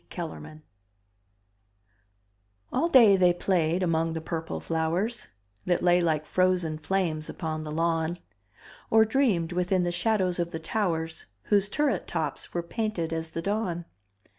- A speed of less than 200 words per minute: Yes, average, 140 wpm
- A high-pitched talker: No, medium, 175 Hz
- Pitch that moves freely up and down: No, average, 3.0 semitones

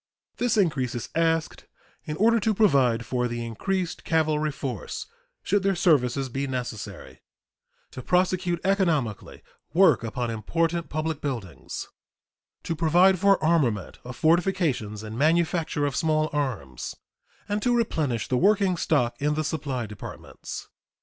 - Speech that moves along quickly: No, slow, 135 wpm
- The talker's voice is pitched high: No, medium, 155 Hz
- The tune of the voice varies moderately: No, wide, 6.2 semitones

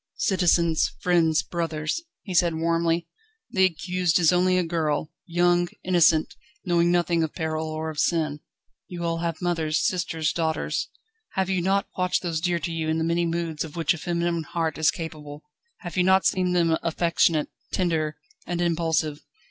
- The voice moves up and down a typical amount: No, narrow, 1.7 semitones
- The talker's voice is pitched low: No, medium, 170 Hz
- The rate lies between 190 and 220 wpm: No, average, 170 wpm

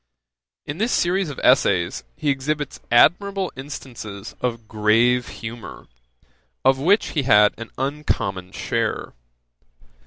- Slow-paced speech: Yes, slow, 115 wpm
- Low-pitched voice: Yes, low, 130 Hz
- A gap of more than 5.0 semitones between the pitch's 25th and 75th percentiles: Yes, wide, 5.5 semitones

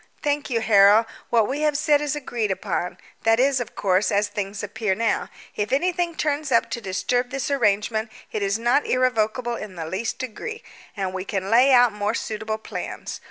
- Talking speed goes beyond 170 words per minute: Yes, average, 190 wpm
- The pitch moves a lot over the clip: No, average, 4.4 semitones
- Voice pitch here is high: Yes, high, 225 Hz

